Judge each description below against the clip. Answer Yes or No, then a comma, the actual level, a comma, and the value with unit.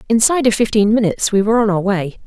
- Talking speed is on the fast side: Yes, fast, 240 wpm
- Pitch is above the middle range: Yes, high, 215 Hz